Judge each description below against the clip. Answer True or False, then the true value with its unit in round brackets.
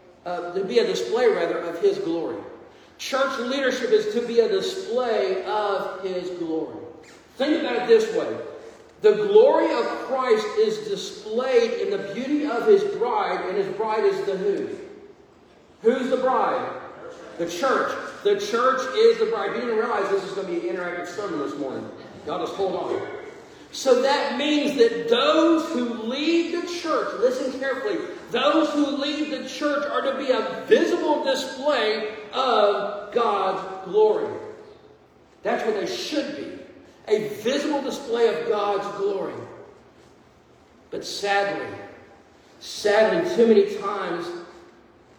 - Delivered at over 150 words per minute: False (145 wpm)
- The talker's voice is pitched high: True (280 Hz)